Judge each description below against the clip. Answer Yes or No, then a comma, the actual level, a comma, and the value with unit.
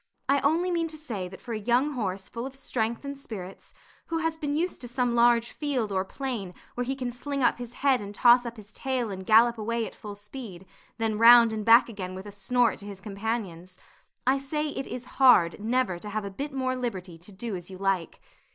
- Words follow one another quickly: Yes, fast, 230 wpm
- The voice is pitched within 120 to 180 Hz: No, high, 235 Hz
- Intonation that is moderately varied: Yes, average, 4.7 semitones